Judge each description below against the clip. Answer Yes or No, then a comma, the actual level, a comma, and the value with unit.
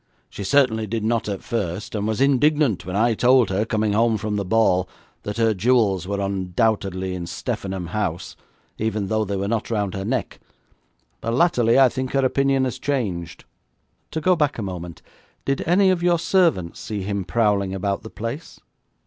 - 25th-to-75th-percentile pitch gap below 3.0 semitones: No, average, 4.6 semitones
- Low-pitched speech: Yes, low, 110 Hz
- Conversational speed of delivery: Yes, average, 185 wpm